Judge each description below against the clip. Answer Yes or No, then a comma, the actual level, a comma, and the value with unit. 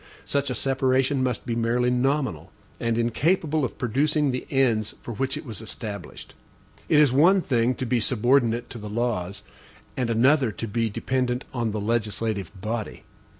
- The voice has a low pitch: Yes, low, 120 Hz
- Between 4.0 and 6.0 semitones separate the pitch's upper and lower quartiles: No, average, 3.0 semitones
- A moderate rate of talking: Yes, average, 165 wpm